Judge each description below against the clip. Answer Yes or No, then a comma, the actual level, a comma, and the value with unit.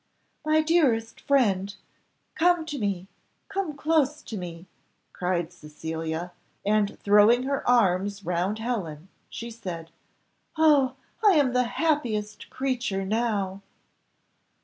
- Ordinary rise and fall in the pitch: No, wide, 6.8 semitones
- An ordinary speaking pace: No, slow, 110 wpm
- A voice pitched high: Yes, high, 220 Hz